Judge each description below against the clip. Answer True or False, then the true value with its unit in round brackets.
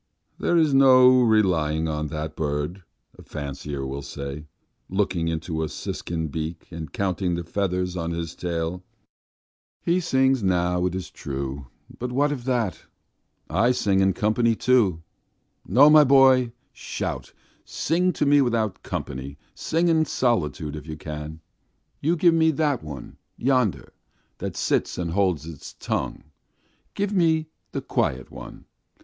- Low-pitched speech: True (90 Hz)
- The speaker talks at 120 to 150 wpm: True (145 wpm)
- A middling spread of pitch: False (8.5 semitones)